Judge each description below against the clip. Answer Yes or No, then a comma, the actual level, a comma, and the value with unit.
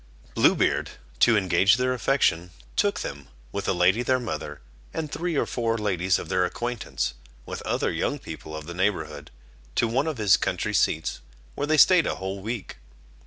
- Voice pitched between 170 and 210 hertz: No, low, 105 Hz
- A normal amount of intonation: No, wide, 6.3 semitones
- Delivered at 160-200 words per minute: Yes, average, 180 wpm